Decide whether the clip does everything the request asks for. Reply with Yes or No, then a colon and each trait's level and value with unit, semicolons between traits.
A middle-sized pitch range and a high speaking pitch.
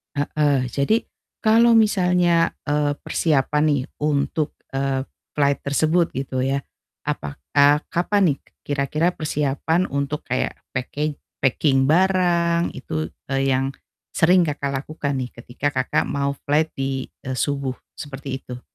No: average, 3.1 semitones; medium, 145 Hz